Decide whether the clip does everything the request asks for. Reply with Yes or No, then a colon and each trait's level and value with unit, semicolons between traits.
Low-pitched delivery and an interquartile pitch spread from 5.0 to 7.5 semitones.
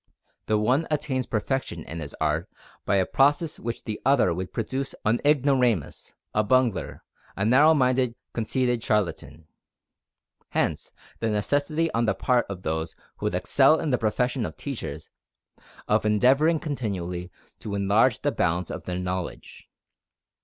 Yes: low, 115 Hz; average, 5.3 semitones